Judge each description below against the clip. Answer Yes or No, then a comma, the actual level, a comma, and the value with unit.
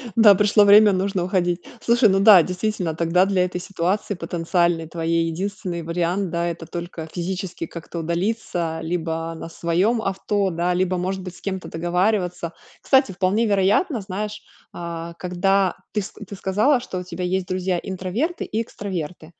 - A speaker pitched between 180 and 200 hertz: Yes, medium, 185 Hz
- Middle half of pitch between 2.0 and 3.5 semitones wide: Yes, average, 2.7 semitones